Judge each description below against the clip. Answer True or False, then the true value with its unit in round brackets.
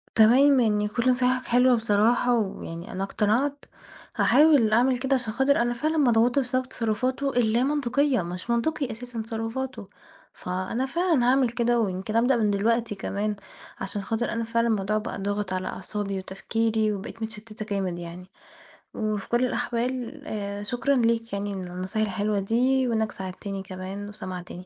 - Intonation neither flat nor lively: True (3.6 semitones)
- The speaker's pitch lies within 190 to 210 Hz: False (225 Hz)